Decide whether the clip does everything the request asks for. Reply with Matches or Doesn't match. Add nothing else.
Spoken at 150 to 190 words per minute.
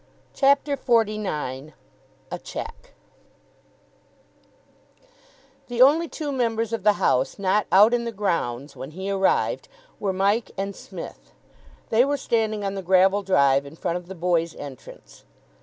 Doesn't match